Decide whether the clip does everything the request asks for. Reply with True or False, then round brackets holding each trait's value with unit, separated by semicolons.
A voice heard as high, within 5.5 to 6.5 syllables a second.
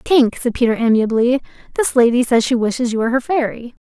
True (245 Hz; 5.9 syllables/s)